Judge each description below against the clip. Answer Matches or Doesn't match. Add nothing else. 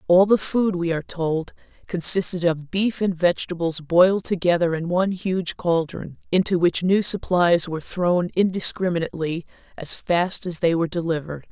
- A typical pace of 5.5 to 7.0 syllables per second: Doesn't match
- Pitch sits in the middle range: Matches